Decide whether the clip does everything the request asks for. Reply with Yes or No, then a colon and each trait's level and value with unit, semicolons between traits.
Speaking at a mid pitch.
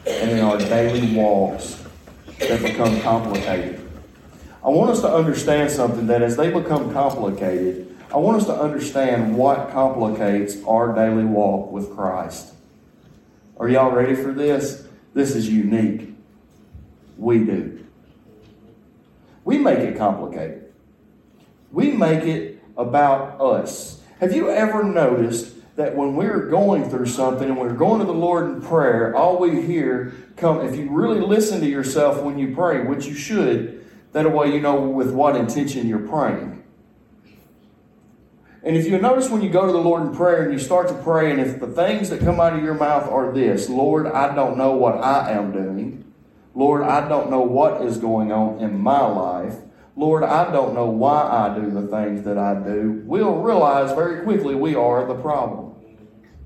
No: low, 130 Hz